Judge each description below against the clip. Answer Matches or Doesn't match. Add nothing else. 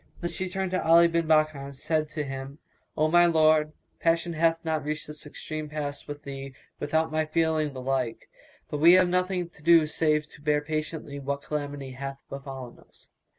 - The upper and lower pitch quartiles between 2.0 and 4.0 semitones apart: Matches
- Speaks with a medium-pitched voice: Matches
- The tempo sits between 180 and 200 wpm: Matches